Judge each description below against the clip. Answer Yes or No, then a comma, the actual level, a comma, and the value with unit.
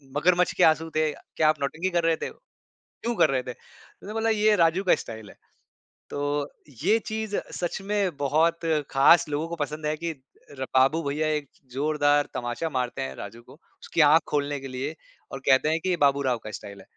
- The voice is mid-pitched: Yes, medium, 155 Hz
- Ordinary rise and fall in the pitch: Yes, average, 3.8 semitones